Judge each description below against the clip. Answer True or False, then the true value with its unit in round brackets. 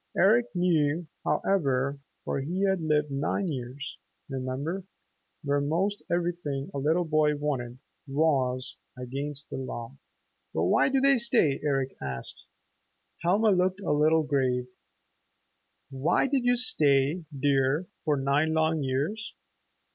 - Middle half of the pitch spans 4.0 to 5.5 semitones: True (4.5 semitones)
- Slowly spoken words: True (125 wpm)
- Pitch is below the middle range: False (150 Hz)